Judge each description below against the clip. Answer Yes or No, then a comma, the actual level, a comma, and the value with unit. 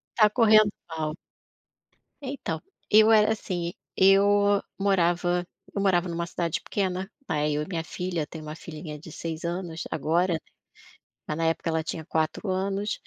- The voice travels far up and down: No, average, 3.6 semitones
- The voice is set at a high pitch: No, medium, 175 Hz